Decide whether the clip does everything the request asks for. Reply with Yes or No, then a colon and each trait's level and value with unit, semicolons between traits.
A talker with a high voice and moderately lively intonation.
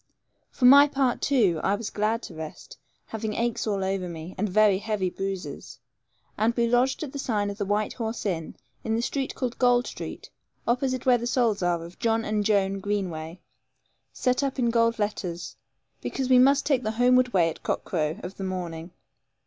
Yes: high, 215 Hz; average, 4.5 semitones